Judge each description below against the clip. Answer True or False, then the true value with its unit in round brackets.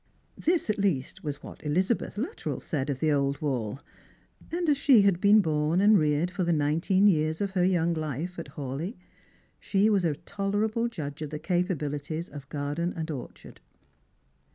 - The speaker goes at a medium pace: True (175 wpm)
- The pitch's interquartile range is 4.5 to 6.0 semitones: True (5.1 semitones)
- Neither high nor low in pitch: True (165 Hz)